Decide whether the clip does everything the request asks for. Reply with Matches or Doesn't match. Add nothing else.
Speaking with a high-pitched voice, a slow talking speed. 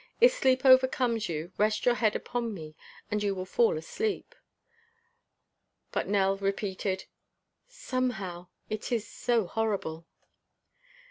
Matches